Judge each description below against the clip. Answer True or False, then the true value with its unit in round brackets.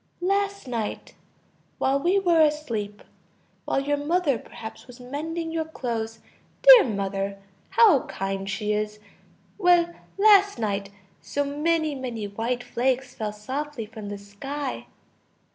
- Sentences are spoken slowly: True (125 wpm)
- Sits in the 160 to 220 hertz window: False (260 Hz)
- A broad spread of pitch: True (7.0 semitones)